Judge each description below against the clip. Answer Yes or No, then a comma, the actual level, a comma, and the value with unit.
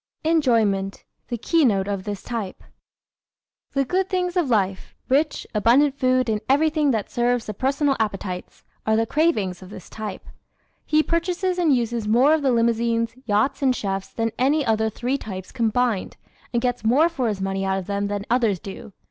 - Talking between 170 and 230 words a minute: Yes, average, 180 wpm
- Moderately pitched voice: No, high, 235 Hz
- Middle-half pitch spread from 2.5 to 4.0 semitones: No, average, 5.2 semitones